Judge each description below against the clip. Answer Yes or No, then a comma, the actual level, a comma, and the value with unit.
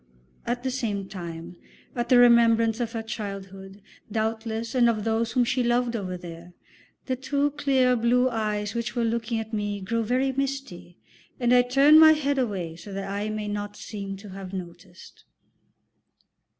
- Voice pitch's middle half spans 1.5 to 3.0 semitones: No, average, 3.8 semitones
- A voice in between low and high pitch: No, high, 225 Hz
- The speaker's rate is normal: Yes, average, 170 wpm